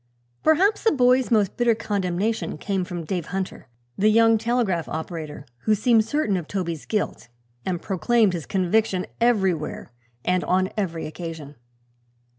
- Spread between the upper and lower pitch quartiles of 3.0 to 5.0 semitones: Yes, average, 4.6 semitones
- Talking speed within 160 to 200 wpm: No, average, 140 wpm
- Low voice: No, high, 195 Hz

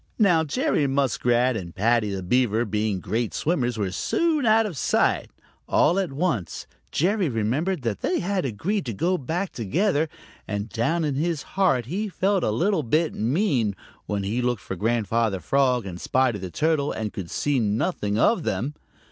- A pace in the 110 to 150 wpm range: No, average, 175 wpm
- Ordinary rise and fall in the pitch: No, wide, 8.0 semitones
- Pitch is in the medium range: No, low, 130 Hz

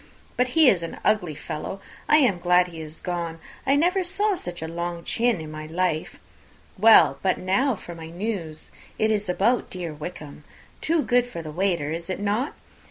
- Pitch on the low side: No, medium, 180 Hz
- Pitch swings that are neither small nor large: No, wide, 6.2 semitones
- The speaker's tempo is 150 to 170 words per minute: No, average, 190 wpm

